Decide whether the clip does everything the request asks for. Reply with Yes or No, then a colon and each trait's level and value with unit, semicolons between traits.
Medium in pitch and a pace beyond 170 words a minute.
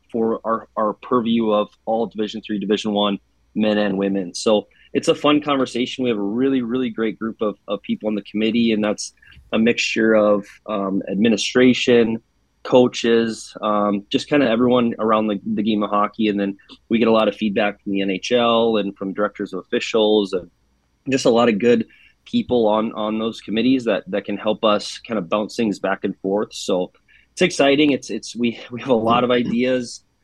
No: low, 110 Hz; average, 200 wpm